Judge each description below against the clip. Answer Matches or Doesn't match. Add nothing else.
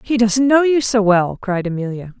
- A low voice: Doesn't match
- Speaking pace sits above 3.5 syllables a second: Matches